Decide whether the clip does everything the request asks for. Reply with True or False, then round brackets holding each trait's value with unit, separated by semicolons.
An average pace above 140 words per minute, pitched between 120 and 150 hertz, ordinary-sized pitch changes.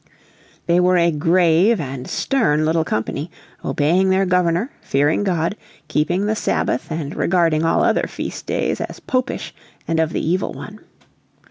False (150 wpm; 170 Hz; 3.2 semitones)